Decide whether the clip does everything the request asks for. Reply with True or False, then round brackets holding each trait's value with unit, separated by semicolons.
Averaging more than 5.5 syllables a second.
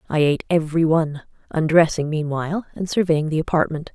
True (6.2 syllables/s)